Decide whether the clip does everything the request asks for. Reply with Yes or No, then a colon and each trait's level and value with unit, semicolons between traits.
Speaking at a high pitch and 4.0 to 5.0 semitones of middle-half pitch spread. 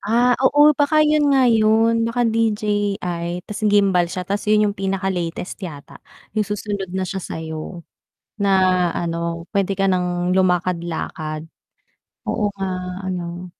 No: high, 195 Hz; average, 3.5 semitones